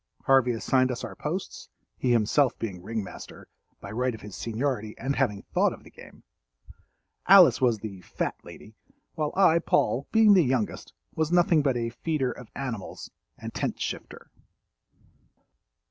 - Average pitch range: Yes, average, 4.7 semitones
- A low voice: Yes, low, 125 Hz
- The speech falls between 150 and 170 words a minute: Yes, average, 155 wpm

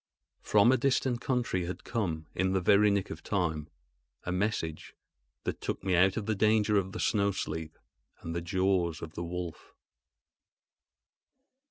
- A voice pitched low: Yes, very low, 95 Hz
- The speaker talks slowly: No, average, 160 wpm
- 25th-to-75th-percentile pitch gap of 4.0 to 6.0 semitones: No, average, 3.6 semitones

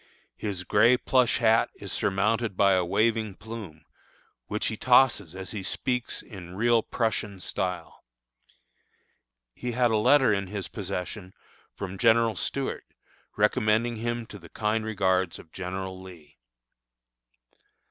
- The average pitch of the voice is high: No, low, 105 Hz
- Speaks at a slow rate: Yes, slow, 130 wpm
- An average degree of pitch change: Yes, average, 3.6 semitones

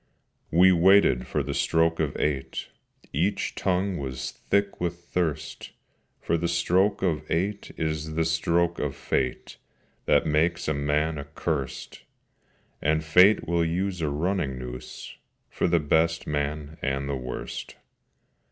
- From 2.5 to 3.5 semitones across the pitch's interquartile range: Yes, average, 3.0 semitones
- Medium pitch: No, very low, 80 Hz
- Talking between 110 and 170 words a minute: Yes, slow, 135 wpm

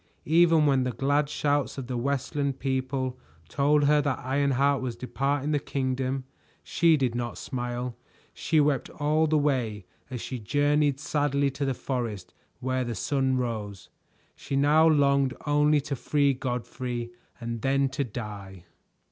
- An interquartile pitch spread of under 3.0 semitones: Yes, narrow, 2.5 semitones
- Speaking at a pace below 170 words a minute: Yes, average, 150 wpm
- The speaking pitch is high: No, low, 135 Hz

